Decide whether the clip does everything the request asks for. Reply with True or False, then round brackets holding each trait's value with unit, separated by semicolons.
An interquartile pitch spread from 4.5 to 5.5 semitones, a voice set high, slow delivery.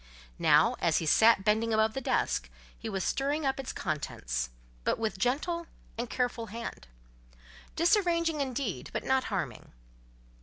False (4.8 semitones; 235 Hz; 145 wpm)